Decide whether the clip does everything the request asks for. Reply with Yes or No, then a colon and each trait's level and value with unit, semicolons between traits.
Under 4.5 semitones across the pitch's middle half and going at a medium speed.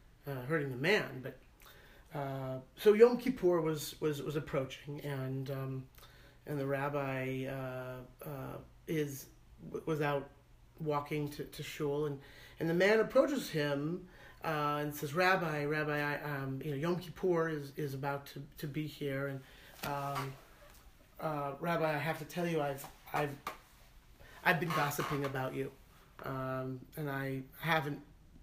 Yes: narrow, 2.5 semitones; average, 150 wpm